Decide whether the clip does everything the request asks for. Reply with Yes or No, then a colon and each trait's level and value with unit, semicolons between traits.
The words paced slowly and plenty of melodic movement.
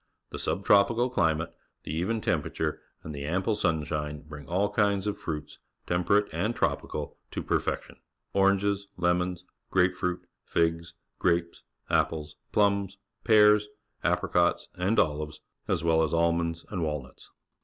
No: slow, 130 wpm; average, 3.7 semitones